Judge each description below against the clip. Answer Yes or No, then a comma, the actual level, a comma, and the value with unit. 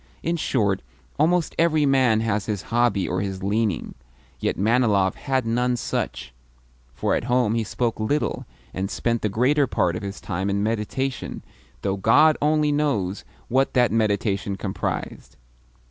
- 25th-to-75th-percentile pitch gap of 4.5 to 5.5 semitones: Yes, average, 4.9 semitones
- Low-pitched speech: Yes, low, 115 Hz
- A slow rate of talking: No, average, 150 wpm